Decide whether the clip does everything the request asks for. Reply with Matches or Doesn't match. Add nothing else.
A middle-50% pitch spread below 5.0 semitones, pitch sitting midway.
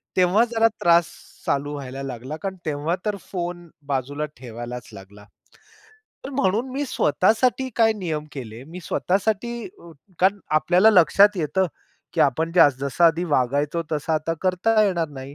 Doesn't match